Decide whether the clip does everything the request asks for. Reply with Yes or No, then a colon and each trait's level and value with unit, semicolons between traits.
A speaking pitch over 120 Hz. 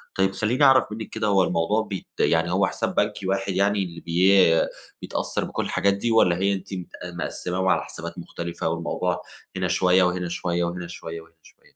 No: very low, 95 Hz